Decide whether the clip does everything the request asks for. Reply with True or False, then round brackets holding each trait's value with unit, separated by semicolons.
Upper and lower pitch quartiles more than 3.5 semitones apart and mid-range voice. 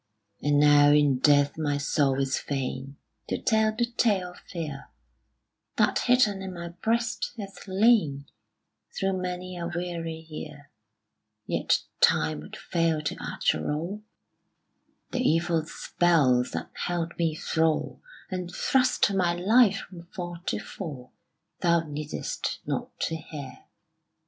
True (4.3 semitones; 170 Hz)